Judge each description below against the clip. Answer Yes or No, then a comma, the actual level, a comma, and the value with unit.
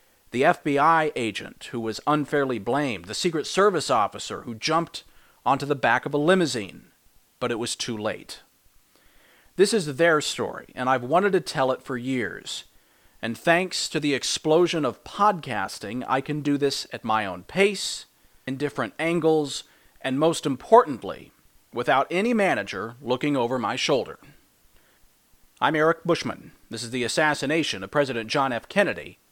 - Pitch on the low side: No, medium, 145 Hz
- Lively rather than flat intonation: No, average, 4.7 semitones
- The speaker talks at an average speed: Yes, average, 155 wpm